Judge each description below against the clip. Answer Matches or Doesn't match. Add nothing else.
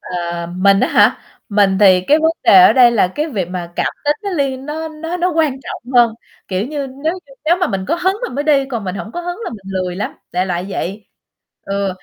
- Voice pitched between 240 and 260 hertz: Matches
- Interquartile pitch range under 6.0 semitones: Doesn't match